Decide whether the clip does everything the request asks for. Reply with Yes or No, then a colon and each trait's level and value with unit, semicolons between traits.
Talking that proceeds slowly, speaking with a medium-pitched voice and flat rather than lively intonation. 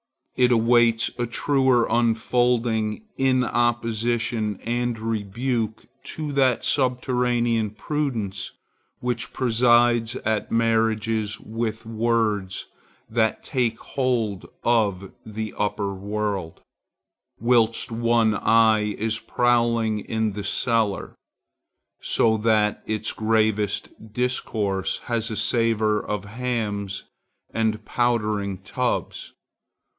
No: slow, 95 wpm; low, 115 Hz; narrow, 2.0 semitones